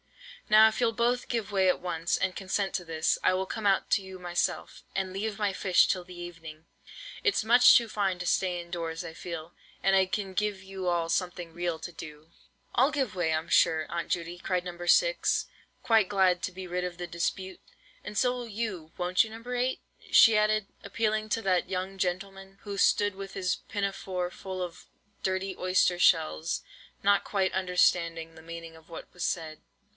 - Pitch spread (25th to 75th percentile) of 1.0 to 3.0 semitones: Yes, average, 2.7 semitones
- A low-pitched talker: No, medium, 185 Hz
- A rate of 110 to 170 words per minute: No, average, 195 wpm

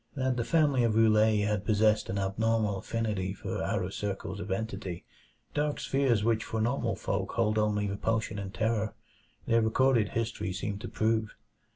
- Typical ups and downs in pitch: No, narrow, 2.1 semitones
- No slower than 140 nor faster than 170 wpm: Yes, average, 165 wpm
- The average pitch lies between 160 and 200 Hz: No, low, 110 Hz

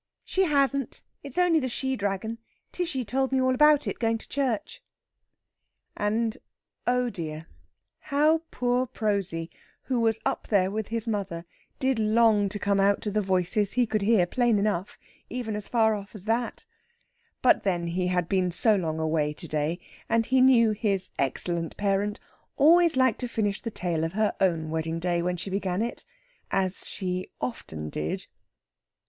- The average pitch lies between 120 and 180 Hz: No, high, 210 Hz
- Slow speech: No, average, 170 wpm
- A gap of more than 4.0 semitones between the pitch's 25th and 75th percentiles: Yes, average, 5.1 semitones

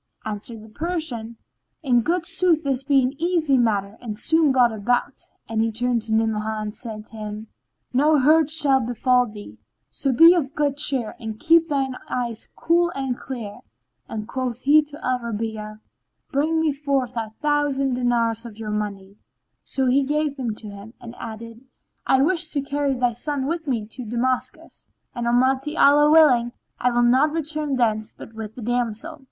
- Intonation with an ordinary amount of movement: Yes, average, 4.5 semitones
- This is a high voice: Yes, very high, 250 Hz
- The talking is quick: No, average, 180 wpm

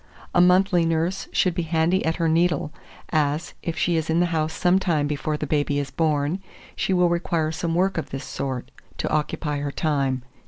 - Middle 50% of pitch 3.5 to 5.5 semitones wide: No, average, 2.9 semitones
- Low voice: No, medium, 160 Hz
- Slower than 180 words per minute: No, average, 200 wpm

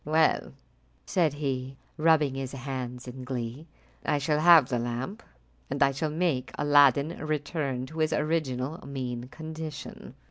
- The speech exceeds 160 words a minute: No, average, 140 wpm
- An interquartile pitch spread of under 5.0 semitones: Yes, average, 3.4 semitones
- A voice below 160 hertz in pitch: Yes, medium, 140 Hz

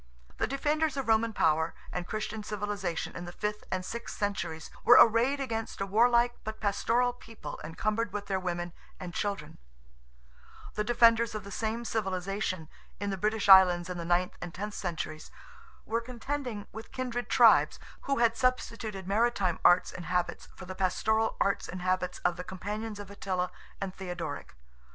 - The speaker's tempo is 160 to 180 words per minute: Yes, average, 165 wpm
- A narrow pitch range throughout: No, average, 3.9 semitones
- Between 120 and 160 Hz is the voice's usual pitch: No, high, 205 Hz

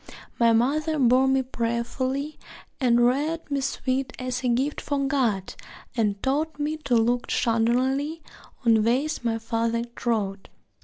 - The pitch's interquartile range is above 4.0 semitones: No, average, 3.2 semitones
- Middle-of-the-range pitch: No, very high, 255 Hz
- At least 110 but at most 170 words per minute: Yes, average, 140 wpm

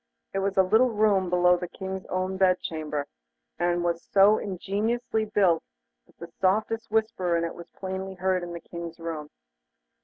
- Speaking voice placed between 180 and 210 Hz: Yes, medium, 185 Hz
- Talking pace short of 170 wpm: No, average, 175 wpm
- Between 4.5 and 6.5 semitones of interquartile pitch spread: No, narrow, 2.6 semitones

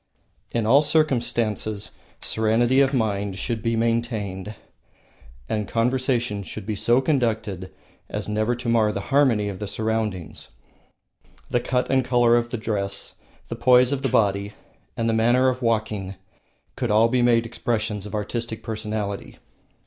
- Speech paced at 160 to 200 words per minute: No, average, 145 wpm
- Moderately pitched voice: No, low, 115 Hz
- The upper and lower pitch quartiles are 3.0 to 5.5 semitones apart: No, narrow, 2.4 semitones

